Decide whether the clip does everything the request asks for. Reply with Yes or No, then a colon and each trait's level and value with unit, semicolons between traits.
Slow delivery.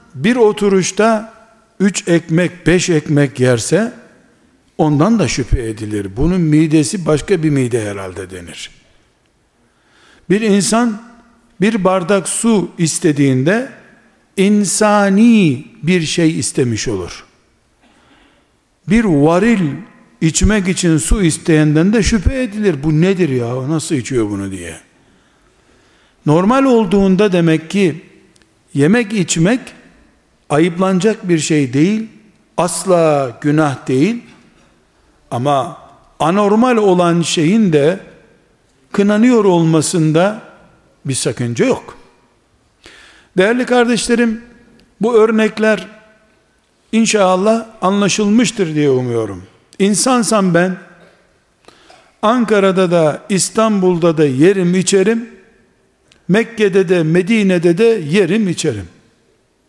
Yes: slow, 90 wpm